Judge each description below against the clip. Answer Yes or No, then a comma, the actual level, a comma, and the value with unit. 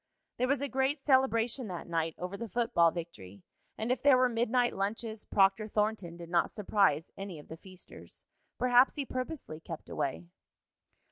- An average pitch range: No, wide, 6.6 semitones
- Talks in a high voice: Yes, high, 215 Hz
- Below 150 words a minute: No, average, 165 wpm